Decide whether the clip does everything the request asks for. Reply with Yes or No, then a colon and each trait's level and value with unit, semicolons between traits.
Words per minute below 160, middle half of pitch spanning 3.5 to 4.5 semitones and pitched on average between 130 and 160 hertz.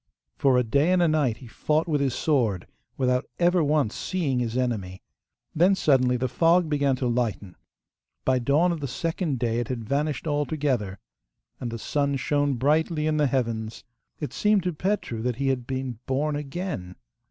No: average, 180 wpm; average, 4.1 semitones; medium, 140 Hz